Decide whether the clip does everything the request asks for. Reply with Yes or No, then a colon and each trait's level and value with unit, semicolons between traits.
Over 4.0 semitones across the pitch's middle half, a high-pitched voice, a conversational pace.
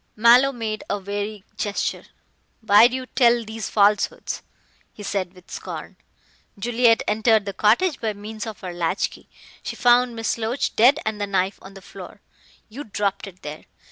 No: average, 2.8 semitones; high, 215 Hz; average, 175 wpm